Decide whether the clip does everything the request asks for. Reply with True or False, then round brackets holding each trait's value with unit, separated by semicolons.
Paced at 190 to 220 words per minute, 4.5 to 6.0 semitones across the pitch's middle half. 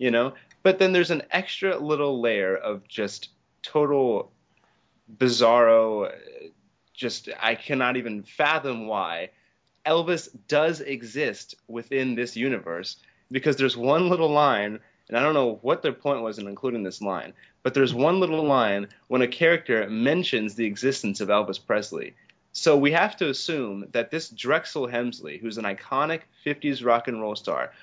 False (155 wpm; 5.0 semitones)